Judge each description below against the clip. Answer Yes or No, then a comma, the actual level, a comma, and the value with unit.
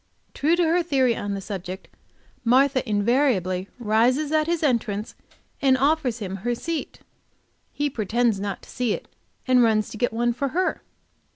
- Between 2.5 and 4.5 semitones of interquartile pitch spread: No, average, 4.9 semitones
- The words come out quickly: No, average, 165 wpm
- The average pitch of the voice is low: No, high, 245 Hz